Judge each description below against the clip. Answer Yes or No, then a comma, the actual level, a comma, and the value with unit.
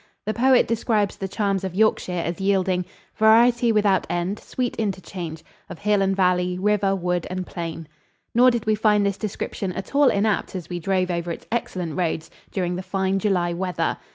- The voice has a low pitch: No, high, 195 Hz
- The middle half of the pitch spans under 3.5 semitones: Yes, average, 2.9 semitones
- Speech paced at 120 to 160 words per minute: No, average, 180 wpm